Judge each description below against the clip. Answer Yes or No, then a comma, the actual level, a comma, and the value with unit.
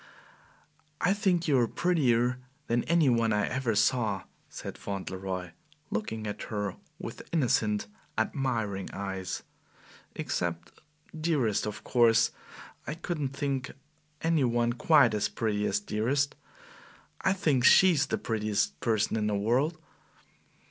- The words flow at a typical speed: No, slow, 125 wpm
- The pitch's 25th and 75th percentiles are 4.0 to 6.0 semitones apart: Yes, wide, 5.4 semitones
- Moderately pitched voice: No, low, 120 Hz